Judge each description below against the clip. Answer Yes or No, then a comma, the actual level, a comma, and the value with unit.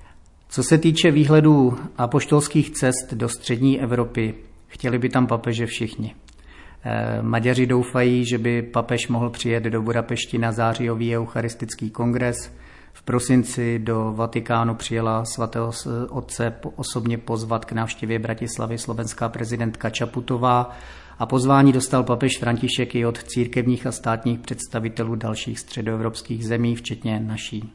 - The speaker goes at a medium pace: Yes, average, 125 wpm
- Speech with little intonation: Yes, narrow, 1.6 semitones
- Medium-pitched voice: No, low, 120 Hz